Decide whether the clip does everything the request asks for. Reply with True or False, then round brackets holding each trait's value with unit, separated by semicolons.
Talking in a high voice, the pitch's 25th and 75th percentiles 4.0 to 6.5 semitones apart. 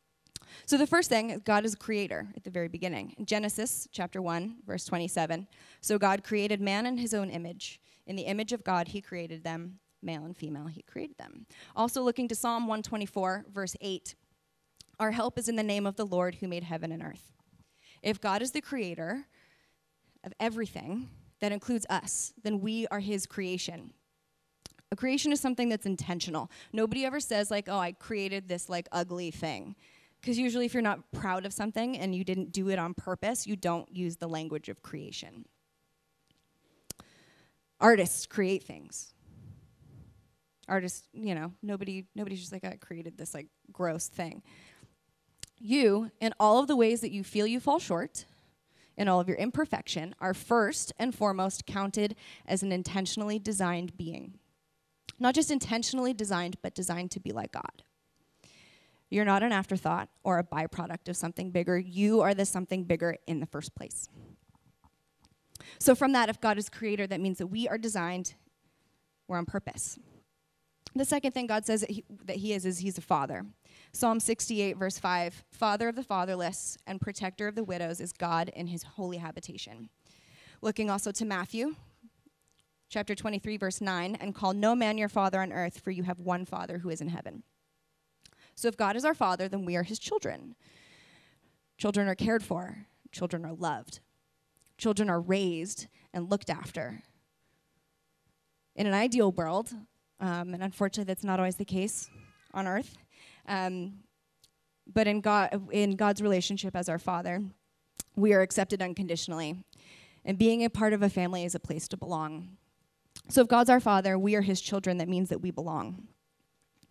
False (195 Hz; 3.4 semitones)